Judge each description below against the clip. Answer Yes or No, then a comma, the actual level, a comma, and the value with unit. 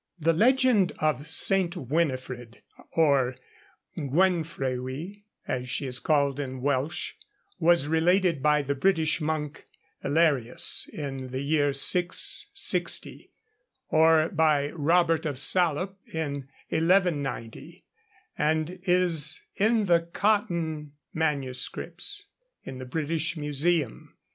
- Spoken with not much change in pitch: No, average, 3.6 semitones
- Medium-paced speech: No, slow, 100 wpm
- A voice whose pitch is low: No, medium, 155 Hz